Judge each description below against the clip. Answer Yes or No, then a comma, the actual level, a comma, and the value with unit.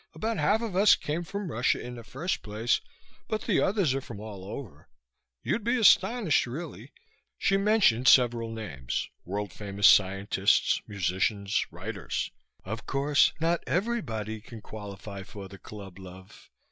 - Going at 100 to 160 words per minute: Yes, average, 145 wpm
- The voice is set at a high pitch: No, low, 115 Hz